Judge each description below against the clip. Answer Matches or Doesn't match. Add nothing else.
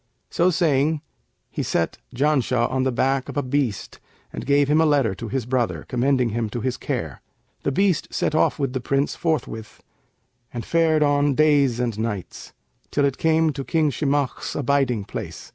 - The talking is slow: Doesn't match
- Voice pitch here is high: Doesn't match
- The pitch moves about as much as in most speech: Matches